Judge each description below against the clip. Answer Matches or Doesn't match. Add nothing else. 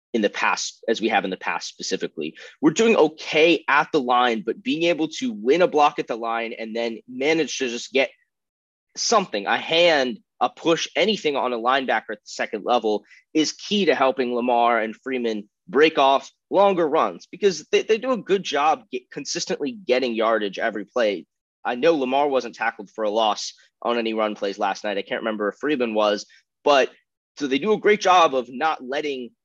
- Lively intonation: Matches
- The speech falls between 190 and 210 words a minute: Matches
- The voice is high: Doesn't match